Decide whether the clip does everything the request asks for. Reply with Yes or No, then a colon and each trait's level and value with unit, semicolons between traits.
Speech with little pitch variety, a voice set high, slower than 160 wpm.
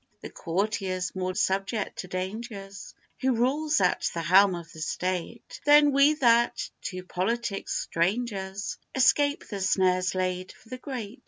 No: average, 4.6 semitones; high, 195 Hz; average, 145 wpm